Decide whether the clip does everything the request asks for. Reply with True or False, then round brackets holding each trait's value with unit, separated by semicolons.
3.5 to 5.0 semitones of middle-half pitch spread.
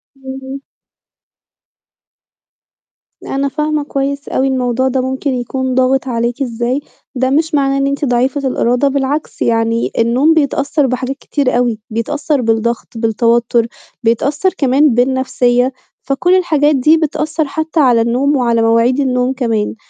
False (2.7 semitones)